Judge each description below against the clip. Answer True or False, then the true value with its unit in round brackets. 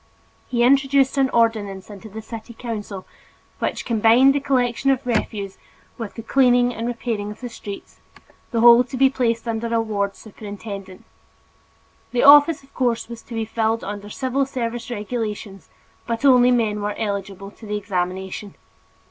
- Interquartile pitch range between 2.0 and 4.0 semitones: True (3.1 semitones)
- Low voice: False (230 Hz)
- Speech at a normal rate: True (160 wpm)